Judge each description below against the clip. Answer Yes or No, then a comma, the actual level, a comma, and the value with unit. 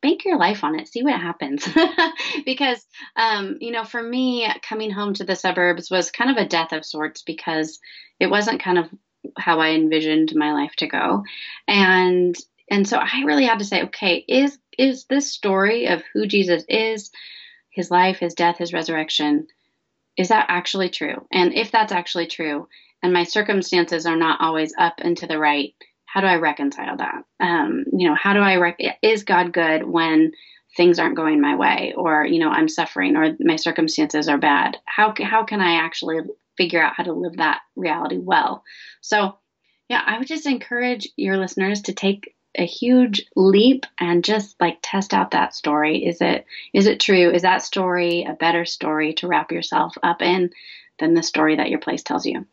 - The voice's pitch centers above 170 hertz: Yes, medium, 185 Hz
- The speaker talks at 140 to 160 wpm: No, average, 195 wpm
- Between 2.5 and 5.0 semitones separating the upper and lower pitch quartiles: No, wide, 5.5 semitones